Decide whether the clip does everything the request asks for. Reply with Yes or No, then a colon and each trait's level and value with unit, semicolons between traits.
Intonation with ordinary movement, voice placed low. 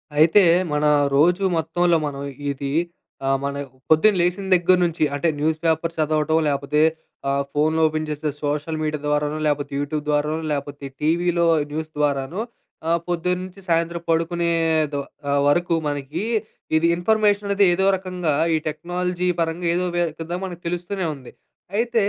No: average, 3.0 semitones; medium, 160 Hz